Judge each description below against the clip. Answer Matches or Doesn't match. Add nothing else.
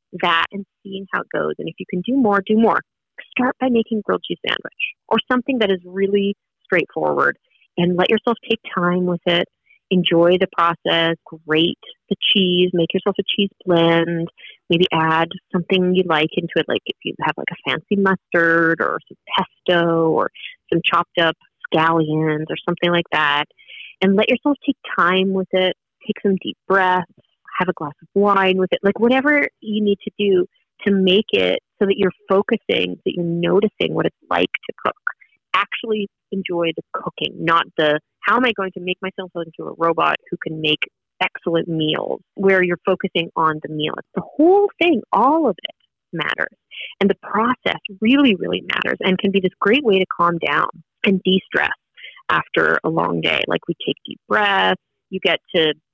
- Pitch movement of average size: Matches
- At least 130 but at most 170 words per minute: Doesn't match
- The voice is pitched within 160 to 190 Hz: Matches